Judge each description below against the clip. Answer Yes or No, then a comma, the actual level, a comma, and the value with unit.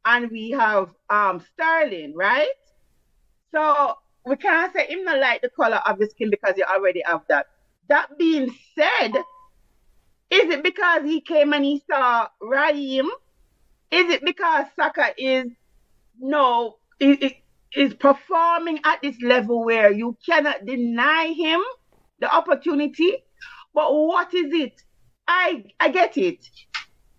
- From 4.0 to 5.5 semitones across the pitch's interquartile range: Yes, average, 4.9 semitones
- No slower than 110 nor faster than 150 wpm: Yes, slow, 135 wpm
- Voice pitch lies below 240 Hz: No, very high, 295 Hz